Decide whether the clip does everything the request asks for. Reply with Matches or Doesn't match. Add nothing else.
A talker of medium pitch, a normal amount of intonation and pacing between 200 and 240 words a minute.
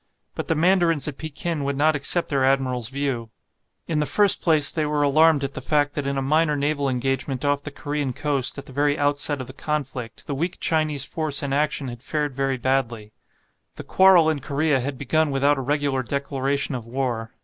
Doesn't match